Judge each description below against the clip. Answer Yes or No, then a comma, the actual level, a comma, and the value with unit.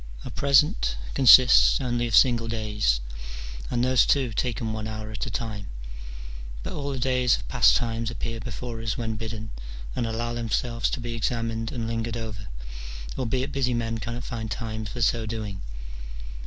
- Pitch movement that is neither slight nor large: No, narrow, 1.8 semitones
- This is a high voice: No, low, 115 Hz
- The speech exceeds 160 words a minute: Yes, average, 170 wpm